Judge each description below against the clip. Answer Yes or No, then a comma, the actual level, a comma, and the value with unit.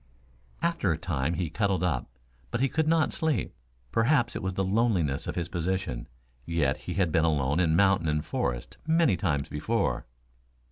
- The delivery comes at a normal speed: Yes, average, 170 wpm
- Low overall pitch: Yes, very low, 90 Hz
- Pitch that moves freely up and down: Yes, wide, 6.0 semitones